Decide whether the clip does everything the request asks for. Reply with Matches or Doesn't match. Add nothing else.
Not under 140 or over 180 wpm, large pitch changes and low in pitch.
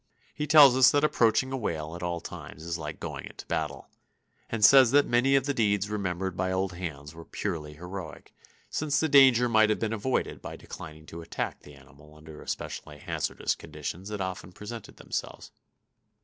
Doesn't match